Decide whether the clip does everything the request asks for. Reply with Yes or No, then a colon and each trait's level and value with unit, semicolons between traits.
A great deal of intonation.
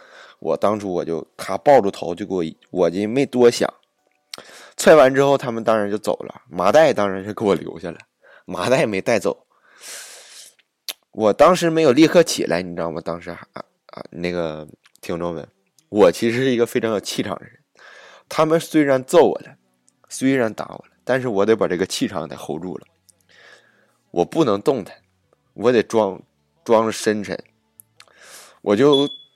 Yes: wide, 8.2 semitones